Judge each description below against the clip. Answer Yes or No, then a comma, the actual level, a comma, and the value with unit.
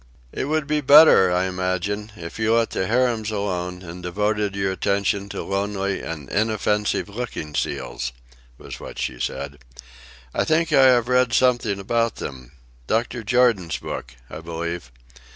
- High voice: No, low, 100 Hz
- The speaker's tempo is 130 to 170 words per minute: Yes, average, 150 wpm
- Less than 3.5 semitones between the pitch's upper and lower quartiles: No, average, 4.7 semitones